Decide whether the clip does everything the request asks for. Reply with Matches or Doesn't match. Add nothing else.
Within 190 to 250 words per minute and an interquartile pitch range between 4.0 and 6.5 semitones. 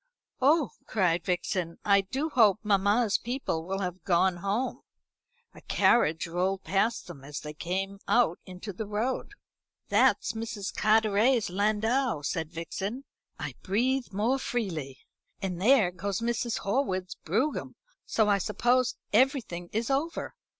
Doesn't match